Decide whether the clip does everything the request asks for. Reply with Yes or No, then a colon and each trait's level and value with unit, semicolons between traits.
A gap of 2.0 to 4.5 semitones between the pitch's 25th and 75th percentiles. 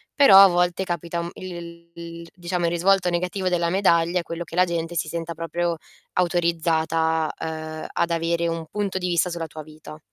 No: narrow, 1.2 semitones